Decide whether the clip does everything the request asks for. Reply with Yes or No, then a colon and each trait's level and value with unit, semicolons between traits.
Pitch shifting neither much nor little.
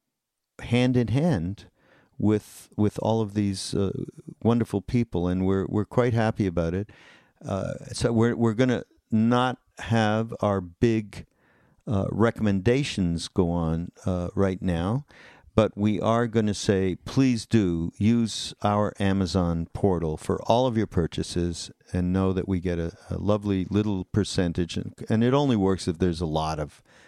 Yes: average, 4.0 semitones